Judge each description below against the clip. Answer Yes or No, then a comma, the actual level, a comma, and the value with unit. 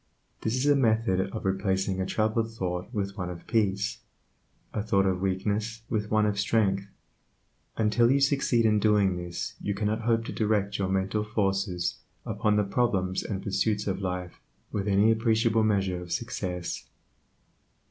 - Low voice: Yes, low, 105 Hz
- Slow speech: No, average, 160 wpm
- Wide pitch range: No, narrow, 2.5 semitones